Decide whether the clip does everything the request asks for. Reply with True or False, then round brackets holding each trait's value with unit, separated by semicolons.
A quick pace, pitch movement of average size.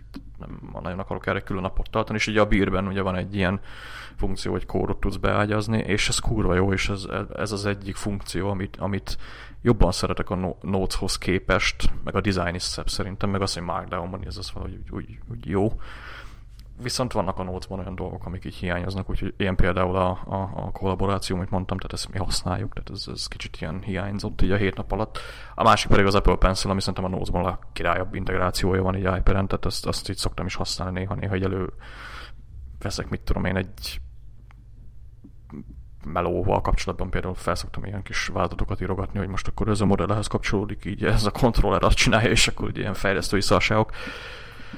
False (195 wpm; 1.8 semitones)